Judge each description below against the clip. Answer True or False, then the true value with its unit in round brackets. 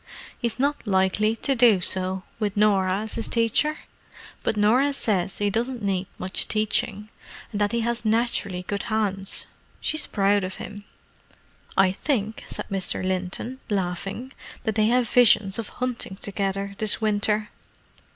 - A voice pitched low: False (210 Hz)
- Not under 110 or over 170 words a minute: True (150 wpm)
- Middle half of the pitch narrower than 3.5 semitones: True (3.0 semitones)